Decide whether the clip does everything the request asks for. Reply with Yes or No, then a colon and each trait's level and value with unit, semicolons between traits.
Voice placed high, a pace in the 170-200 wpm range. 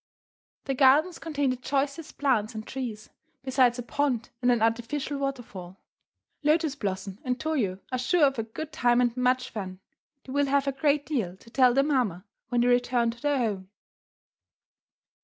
Yes: very high, 255 Hz; average, 175 wpm